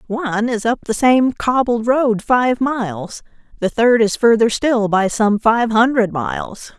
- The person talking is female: Yes, female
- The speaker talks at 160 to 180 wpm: Yes, average, 170 wpm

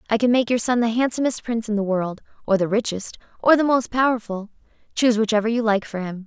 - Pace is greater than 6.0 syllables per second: Yes, 6.3 syllables/s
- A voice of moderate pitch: No, high, 225 Hz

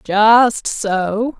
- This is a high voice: Yes, high, 215 Hz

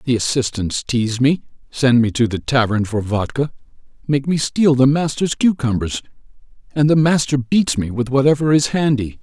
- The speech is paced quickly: No, average, 170 wpm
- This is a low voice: Yes, low, 130 Hz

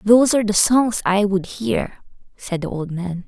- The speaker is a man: No, female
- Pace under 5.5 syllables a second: Yes, 4.7 syllables/s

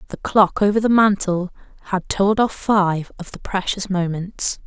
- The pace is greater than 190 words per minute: No, average, 165 wpm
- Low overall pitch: No, high, 195 Hz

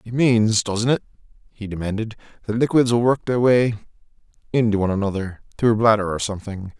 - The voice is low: Yes, low, 110 Hz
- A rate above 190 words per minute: No, average, 170 wpm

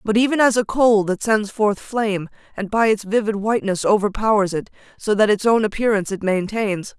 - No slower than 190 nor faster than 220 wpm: Yes, average, 200 wpm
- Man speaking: No, female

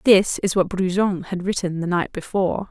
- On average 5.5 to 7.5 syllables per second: No, 5.1 syllables/s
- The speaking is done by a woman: Yes, female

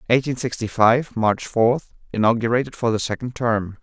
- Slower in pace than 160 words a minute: Yes, average, 140 wpm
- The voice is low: Yes, low, 115 Hz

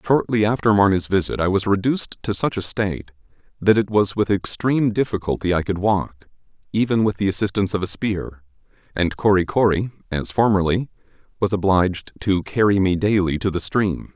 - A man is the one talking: Yes, male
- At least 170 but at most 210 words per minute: Yes, average, 175 wpm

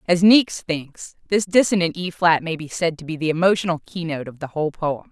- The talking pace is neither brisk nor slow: No, fast, 225 wpm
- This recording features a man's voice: No, female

